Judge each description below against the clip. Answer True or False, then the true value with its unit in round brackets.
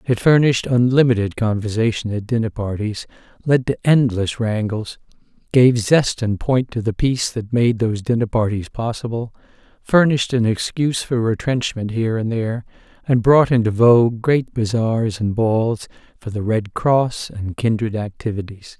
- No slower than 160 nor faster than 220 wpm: False (150 wpm)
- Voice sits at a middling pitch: False (115 Hz)